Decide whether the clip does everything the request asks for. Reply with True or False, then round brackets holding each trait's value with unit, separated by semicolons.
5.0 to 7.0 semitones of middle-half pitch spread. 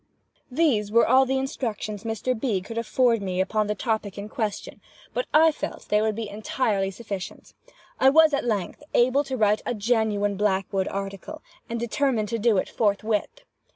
False (3.6 semitones)